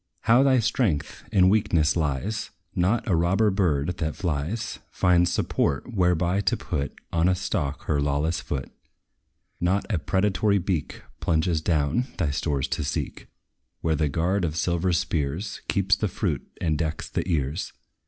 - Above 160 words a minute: No, average, 155 wpm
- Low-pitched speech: Yes, very low, 85 Hz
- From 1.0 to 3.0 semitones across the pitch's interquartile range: No, average, 4.2 semitones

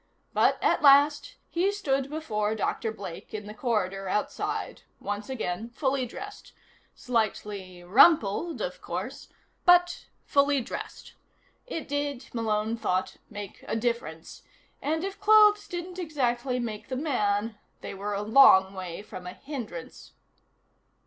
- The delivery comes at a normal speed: No, slow, 130 wpm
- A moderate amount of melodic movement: No, wide, 6.2 semitones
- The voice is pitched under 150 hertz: No, high, 235 Hz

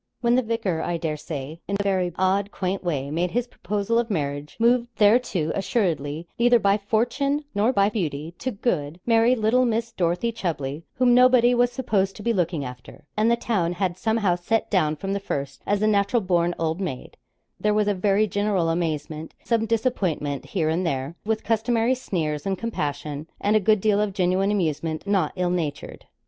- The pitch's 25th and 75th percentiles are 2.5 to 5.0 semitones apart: No, wide, 5.4 semitones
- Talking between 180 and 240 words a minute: Yes, average, 190 wpm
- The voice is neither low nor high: No, high, 195 Hz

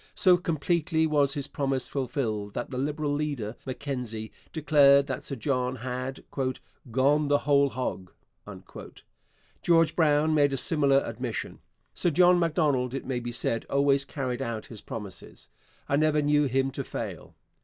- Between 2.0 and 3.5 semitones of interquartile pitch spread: Yes, average, 2.9 semitones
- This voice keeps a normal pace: Yes, average, 150 wpm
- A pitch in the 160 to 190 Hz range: No, medium, 140 Hz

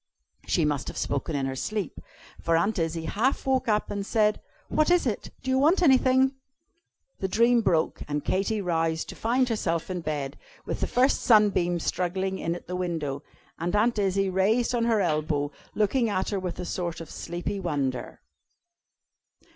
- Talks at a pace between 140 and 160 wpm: No, average, 180 wpm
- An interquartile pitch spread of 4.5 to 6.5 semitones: Yes, average, 5.3 semitones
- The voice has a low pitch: No, high, 190 Hz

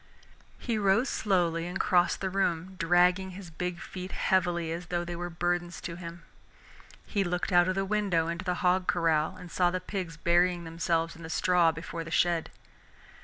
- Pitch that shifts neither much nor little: No, narrow, 1.7 semitones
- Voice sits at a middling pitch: Yes, medium, 175 Hz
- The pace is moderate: Yes, average, 185 wpm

